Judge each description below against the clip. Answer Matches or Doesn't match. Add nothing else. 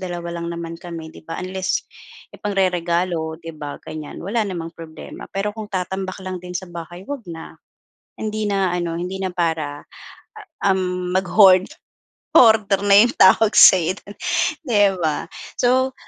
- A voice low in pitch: Doesn't match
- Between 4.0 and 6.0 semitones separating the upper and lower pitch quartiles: Doesn't match